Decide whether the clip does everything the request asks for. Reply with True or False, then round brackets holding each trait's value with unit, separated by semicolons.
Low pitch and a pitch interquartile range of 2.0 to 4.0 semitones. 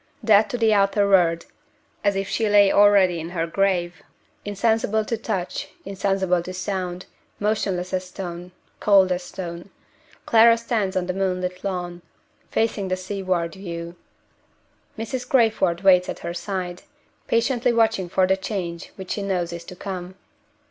False (190 Hz; 2.4 semitones)